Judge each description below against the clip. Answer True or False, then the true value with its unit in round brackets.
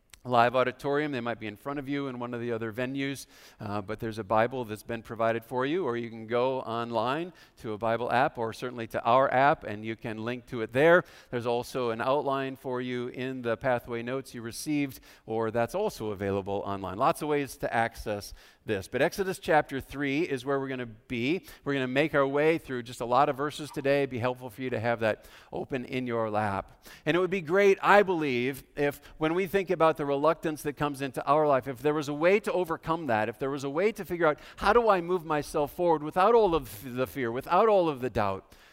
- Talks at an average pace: False (240 wpm)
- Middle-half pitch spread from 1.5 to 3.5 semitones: False (4.3 semitones)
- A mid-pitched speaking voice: False (130 Hz)